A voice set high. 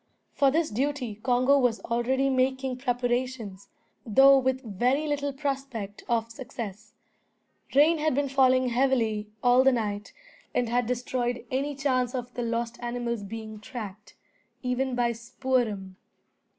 Yes: high, 245 Hz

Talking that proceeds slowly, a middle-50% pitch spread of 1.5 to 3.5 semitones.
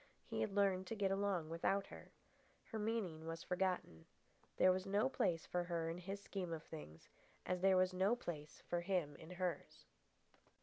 No: average, 180 wpm; average, 2.9 semitones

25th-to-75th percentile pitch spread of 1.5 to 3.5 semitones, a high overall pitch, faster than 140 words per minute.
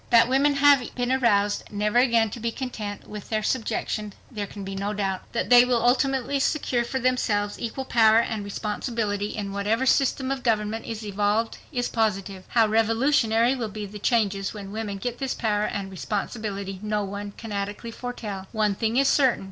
Yes: average, 3.1 semitones; high, 220 Hz; average, 185 wpm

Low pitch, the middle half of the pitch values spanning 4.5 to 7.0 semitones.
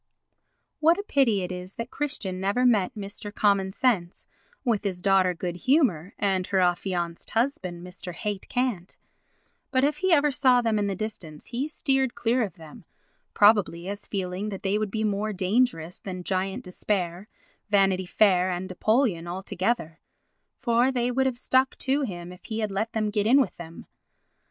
No: high, 200 Hz; average, 4.9 semitones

